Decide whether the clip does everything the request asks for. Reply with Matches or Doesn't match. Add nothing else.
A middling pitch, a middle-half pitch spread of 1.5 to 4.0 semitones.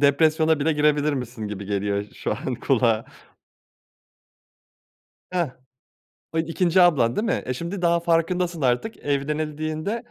Doesn't match